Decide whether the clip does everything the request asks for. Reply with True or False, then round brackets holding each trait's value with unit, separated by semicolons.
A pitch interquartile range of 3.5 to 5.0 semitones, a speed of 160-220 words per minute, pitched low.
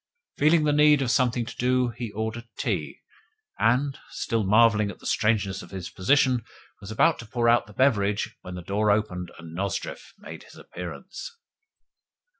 True (4.1 semitones; 170 wpm; 115 Hz)